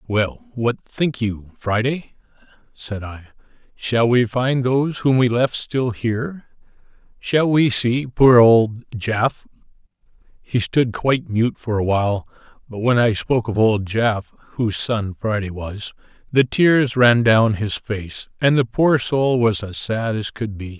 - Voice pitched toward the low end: Yes, low, 115 Hz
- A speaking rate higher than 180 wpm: No, average, 170 wpm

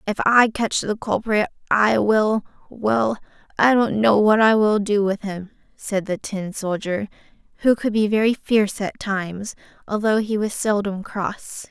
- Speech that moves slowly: No, average, 165 wpm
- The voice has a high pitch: Yes, high, 210 Hz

